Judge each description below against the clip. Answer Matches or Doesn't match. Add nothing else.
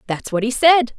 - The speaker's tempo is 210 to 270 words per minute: Matches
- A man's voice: Doesn't match